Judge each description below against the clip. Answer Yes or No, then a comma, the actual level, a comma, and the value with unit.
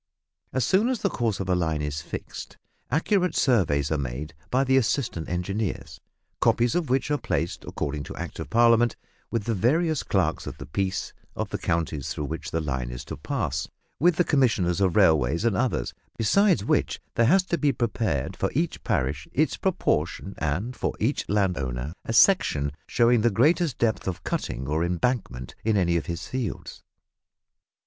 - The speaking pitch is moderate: No, low, 100 Hz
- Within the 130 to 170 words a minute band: No, average, 180 wpm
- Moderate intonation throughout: No, wide, 8.7 semitones